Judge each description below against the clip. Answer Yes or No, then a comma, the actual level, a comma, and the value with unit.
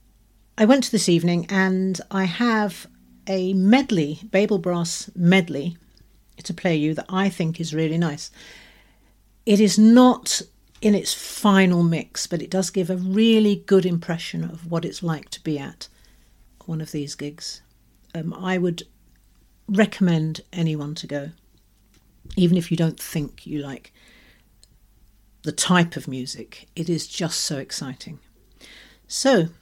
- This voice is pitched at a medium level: Yes, medium, 170 Hz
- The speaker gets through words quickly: No, average, 145 wpm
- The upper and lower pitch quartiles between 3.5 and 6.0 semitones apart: Yes, average, 4.0 semitones